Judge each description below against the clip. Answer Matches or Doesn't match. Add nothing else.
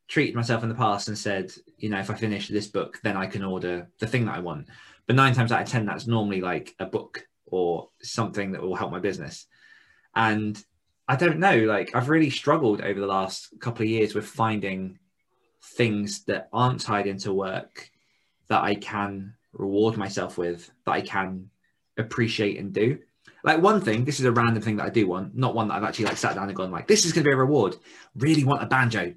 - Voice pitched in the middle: Doesn't match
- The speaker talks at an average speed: Doesn't match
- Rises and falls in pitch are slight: Doesn't match